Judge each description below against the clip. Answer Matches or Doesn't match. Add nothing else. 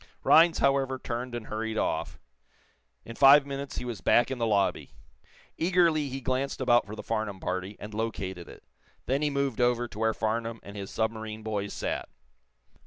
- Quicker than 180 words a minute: Doesn't match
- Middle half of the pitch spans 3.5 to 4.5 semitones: Matches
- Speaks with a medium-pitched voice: Doesn't match